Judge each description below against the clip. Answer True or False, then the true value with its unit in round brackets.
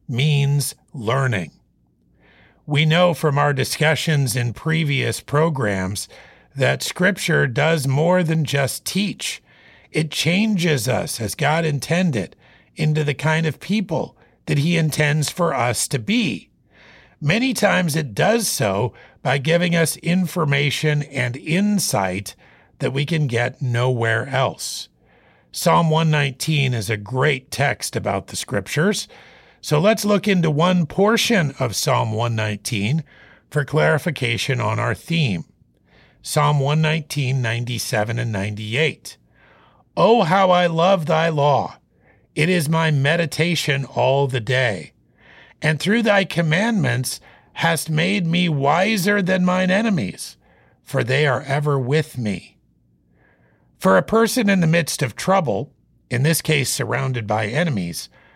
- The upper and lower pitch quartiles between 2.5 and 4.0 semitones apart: False (5.2 semitones)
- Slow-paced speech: True (125 wpm)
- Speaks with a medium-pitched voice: True (150 Hz)